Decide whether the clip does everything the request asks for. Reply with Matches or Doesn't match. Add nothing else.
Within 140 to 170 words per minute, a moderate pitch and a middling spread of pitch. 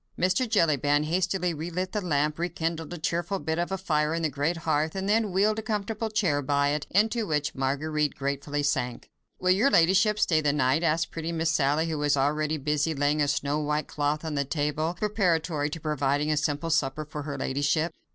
Doesn't match